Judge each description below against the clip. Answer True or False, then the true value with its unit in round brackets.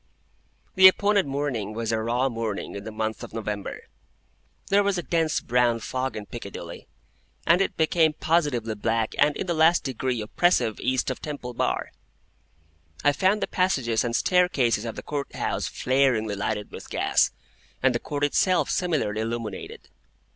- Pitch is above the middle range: False (130 Hz)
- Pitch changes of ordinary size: False (6.2 semitones)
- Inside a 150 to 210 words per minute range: True (160 wpm)